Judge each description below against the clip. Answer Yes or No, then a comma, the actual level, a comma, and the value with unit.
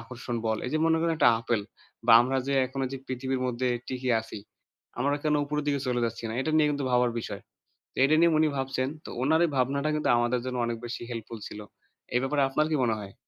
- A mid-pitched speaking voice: No, low, 130 Hz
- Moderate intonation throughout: Yes, average, 3.3 semitones